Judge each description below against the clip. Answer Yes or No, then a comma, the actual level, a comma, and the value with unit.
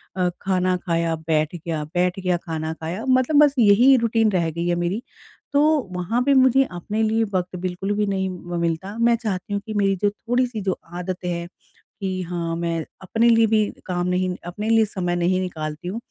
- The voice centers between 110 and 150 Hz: No, medium, 185 Hz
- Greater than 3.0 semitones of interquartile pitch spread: Yes, average, 4.0 semitones